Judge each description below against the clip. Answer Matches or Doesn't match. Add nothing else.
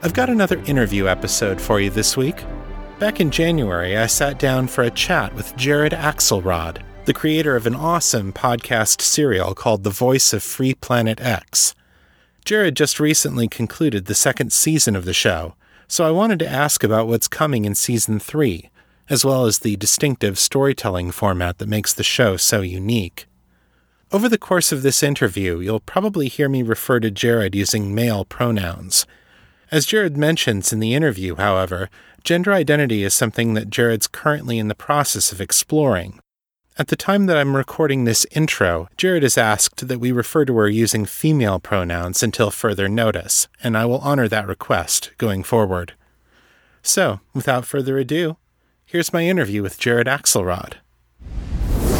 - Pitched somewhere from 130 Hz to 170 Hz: Doesn't match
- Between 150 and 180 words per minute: Matches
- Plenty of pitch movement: Matches